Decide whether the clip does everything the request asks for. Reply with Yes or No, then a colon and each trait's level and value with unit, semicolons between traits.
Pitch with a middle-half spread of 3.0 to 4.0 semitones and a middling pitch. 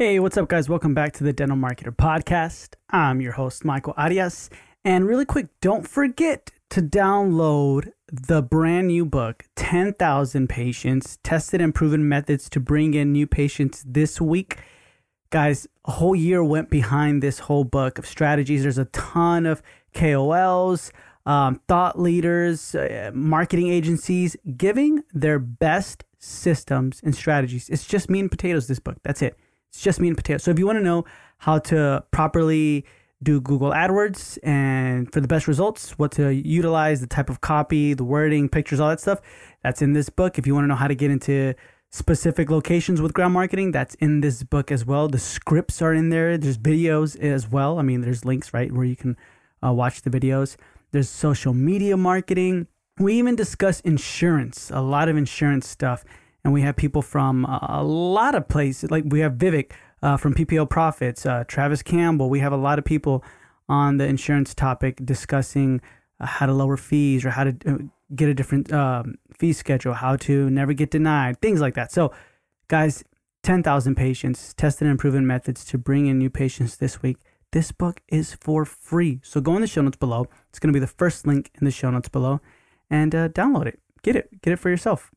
Yes: average, 3.5 semitones; medium, 145 Hz